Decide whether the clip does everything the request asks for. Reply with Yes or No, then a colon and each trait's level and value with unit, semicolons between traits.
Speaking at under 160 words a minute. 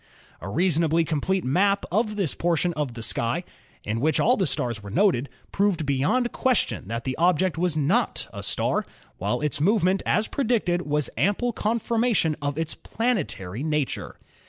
No: average, 165 wpm